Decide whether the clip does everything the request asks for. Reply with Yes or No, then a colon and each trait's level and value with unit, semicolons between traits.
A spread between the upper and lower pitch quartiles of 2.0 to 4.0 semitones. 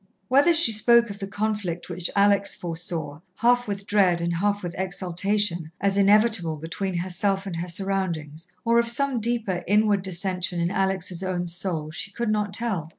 Yes: average, 3.2 semitones